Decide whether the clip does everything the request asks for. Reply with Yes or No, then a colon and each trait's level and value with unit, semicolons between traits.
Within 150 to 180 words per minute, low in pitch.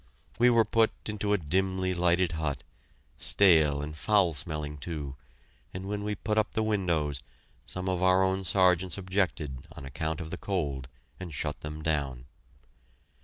Yes: average, 160 wpm; very low, 90 Hz